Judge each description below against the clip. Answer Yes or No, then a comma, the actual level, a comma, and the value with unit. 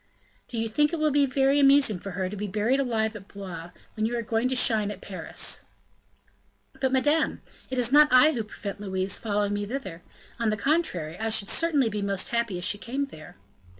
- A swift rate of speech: Yes, fast, 215 wpm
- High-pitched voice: Yes, high, 225 Hz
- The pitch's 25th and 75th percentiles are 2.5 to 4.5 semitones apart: No, average, 5.0 semitones